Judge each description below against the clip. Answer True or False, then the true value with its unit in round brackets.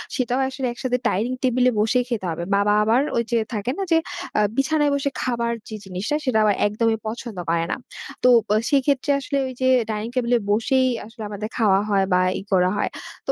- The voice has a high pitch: True (235 Hz)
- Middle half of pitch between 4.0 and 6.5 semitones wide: False (3.6 semitones)